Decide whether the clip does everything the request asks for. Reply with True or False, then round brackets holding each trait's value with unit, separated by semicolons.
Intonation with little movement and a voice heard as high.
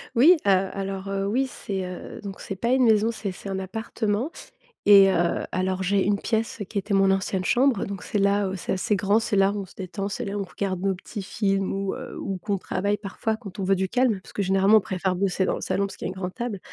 True (1.6 semitones; 195 Hz)